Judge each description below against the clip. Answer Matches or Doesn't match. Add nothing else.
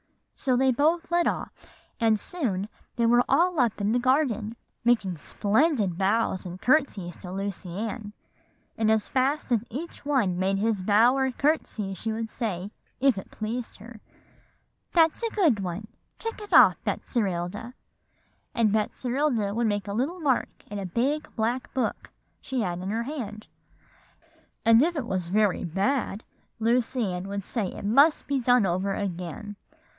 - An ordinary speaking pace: Matches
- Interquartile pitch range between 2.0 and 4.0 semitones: Doesn't match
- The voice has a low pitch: Doesn't match